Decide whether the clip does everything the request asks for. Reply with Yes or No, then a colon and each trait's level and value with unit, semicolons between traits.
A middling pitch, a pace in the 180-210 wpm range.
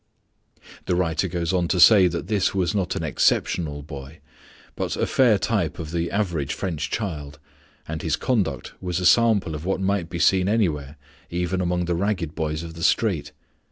No: very low, 85 Hz; average, 185 wpm